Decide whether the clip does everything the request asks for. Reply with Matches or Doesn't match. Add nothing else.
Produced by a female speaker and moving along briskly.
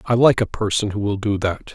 Doesn't match